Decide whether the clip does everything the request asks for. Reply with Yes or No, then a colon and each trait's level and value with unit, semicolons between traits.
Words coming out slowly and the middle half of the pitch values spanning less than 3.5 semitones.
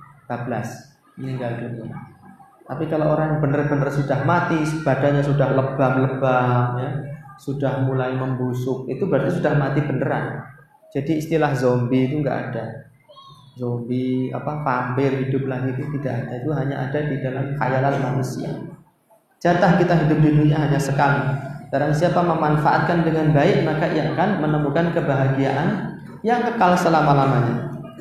No: average, 135 wpm; average, 2.9 semitones